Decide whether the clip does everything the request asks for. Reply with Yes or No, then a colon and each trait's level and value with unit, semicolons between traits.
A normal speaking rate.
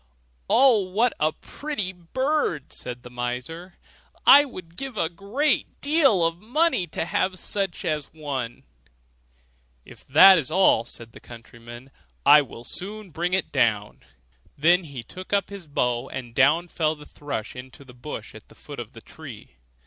Yes: average, 160 wpm